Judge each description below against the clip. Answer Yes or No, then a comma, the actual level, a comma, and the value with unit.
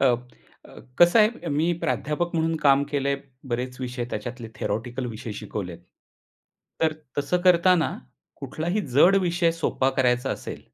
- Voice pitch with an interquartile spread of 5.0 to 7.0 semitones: Yes, wide, 5.5 semitones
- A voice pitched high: No, medium, 140 Hz